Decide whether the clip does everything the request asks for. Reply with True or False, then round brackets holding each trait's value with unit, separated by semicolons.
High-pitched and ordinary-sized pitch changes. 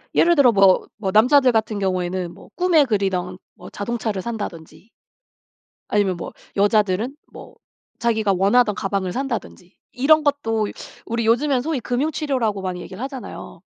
True (220 Hz; 5.0 semitones)